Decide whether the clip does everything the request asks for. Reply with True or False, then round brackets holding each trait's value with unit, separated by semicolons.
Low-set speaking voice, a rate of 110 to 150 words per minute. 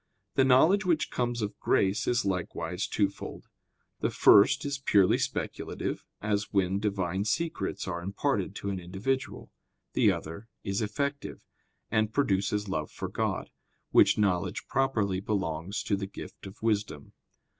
True (100 Hz; 140 wpm)